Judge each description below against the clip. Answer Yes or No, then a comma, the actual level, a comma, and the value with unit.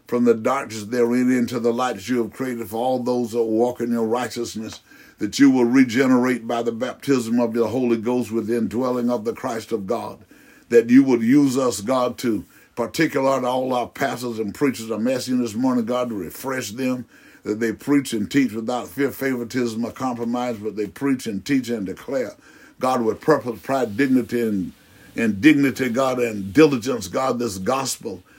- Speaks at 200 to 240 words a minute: No, average, 190 wpm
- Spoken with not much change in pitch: Yes, narrow, 2.3 semitones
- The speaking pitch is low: Yes, low, 125 Hz